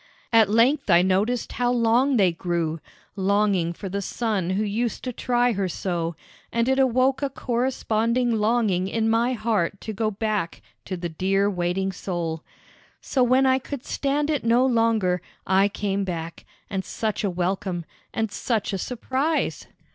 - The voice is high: Yes, high, 215 Hz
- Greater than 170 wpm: No, average, 160 wpm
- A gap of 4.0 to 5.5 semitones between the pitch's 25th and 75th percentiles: Yes, average, 4.5 semitones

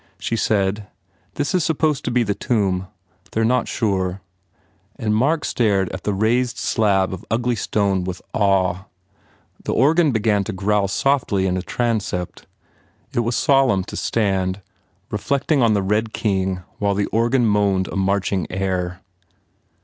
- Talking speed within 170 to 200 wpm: No, average, 155 wpm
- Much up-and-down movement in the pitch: No, average, 3.7 semitones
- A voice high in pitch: No, low, 105 Hz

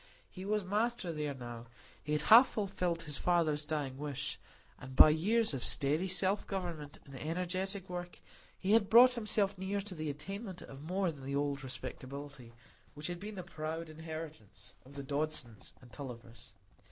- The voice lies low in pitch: No, medium, 160 Hz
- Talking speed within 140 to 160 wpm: No, average, 170 wpm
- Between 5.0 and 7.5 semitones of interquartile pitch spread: Yes, average, 5.3 semitones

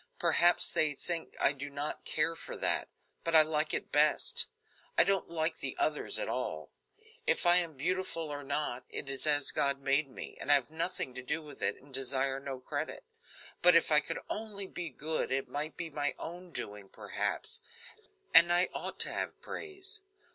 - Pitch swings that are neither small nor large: Yes, average, 3.8 semitones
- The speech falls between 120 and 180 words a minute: No, average, 190 wpm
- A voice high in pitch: No, medium, 155 Hz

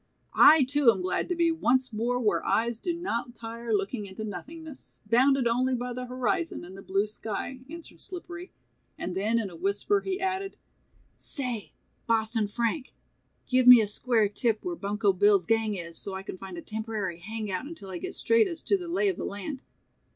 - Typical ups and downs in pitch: No, wide, 5.9 semitones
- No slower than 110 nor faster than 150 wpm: No, average, 195 wpm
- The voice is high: Yes, high, 230 Hz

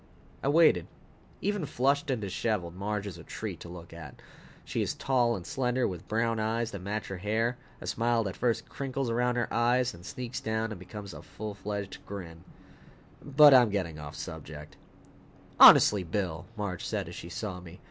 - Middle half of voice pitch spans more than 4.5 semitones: Yes, average, 4.9 semitones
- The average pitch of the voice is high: No, low, 110 Hz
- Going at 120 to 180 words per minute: No, average, 190 wpm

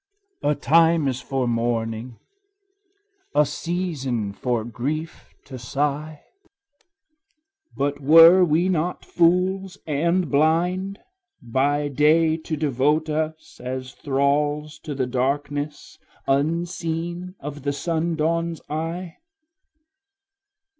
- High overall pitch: No, medium, 150 Hz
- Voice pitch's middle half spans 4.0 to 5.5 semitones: No, average, 3.4 semitones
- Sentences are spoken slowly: Yes, slow, 95 wpm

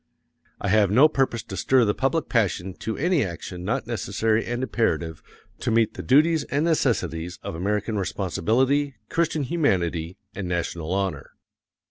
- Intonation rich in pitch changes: Yes, wide, 6.4 semitones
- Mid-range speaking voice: No, low, 110 Hz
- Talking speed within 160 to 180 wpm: No, average, 150 wpm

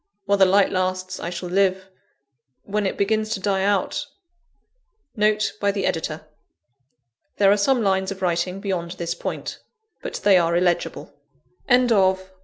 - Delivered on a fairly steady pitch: Yes, narrow, 2.2 semitones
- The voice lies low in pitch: No, high, 190 Hz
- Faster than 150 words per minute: Yes, average, 170 wpm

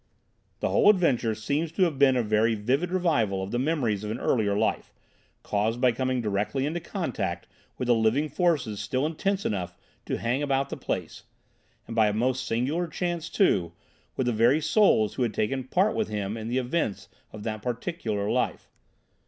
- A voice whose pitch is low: Yes, low, 125 Hz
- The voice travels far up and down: Yes, wide, 6.0 semitones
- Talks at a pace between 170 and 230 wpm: Yes, average, 185 wpm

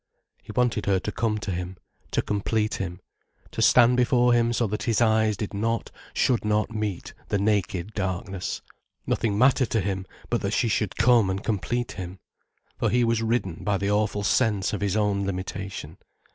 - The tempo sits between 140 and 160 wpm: No, average, 185 wpm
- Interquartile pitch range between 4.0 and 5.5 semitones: No, average, 2.8 semitones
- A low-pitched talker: Yes, low, 105 Hz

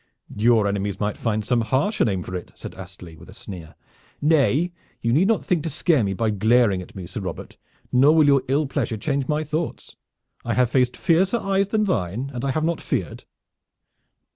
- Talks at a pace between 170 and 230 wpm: Yes, average, 200 wpm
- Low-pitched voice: Yes, low, 125 Hz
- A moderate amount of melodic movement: No, wide, 7.3 semitones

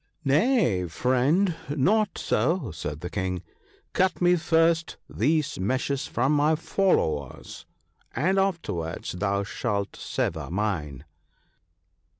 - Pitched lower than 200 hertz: Yes, low, 135 Hz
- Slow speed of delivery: Yes, slow, 115 wpm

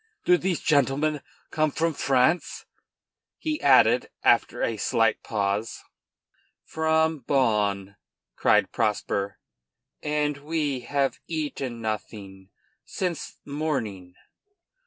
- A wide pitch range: Yes, wide, 6.2 semitones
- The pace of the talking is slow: Yes, slow, 95 wpm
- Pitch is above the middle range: No, medium, 140 Hz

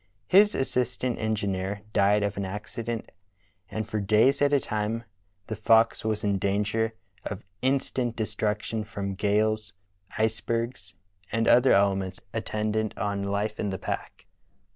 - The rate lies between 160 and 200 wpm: No, average, 140 wpm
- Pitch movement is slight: Yes, narrow, 2.1 semitones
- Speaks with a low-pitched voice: Yes, low, 110 Hz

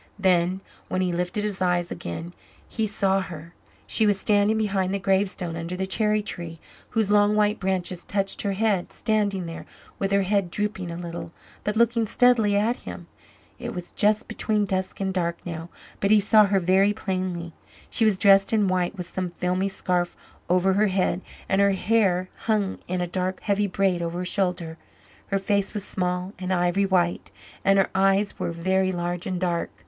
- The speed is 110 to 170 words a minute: No, average, 185 wpm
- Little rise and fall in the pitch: Yes, narrow, 2.3 semitones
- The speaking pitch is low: No, high, 190 Hz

